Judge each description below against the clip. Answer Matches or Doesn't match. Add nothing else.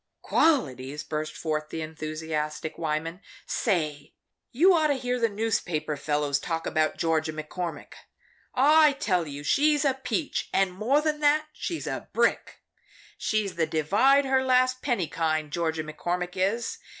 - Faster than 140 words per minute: Matches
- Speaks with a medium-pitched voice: Matches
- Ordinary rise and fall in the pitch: Doesn't match